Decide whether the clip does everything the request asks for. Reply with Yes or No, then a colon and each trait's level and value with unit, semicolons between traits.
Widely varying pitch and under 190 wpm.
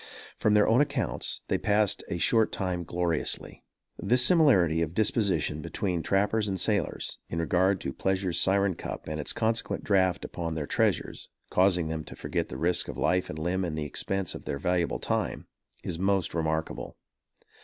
No: average, 3.6 semitones; average, 175 wpm